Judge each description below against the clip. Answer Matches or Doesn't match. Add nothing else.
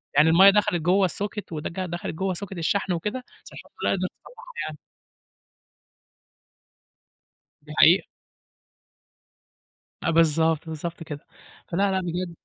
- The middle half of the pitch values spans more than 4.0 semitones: Doesn't match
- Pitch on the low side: Doesn't match